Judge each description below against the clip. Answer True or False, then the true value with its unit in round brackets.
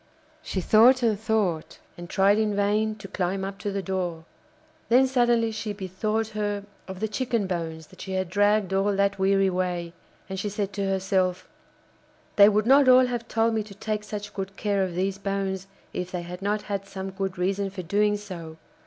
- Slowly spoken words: False (200 wpm)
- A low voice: False (200 Hz)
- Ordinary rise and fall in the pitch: False (2.1 semitones)